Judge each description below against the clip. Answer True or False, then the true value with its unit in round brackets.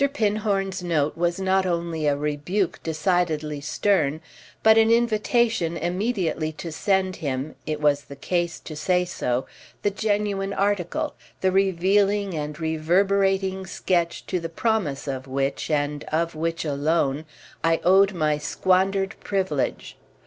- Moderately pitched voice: True (175 Hz)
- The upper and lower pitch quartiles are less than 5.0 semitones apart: True (4.1 semitones)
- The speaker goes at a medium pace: False (125 wpm)